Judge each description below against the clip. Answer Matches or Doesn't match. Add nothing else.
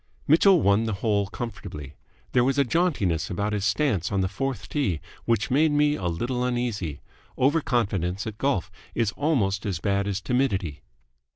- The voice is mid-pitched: Doesn't match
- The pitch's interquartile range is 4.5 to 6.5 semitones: Matches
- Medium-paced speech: Matches